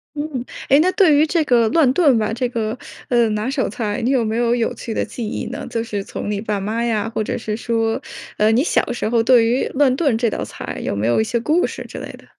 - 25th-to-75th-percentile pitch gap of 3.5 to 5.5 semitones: No, average, 3.1 semitones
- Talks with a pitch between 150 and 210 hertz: No, high, 235 Hz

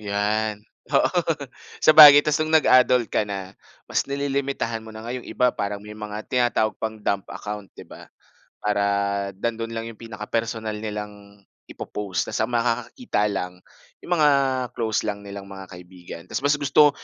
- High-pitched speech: No, low, 110 Hz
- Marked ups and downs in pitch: No, average, 3.6 semitones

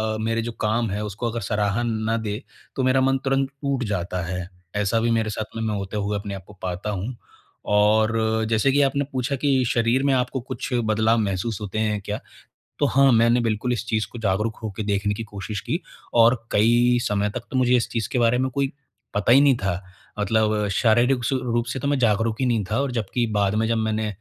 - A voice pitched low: Yes, low, 110 Hz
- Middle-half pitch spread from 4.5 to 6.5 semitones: No, average, 2.9 semitones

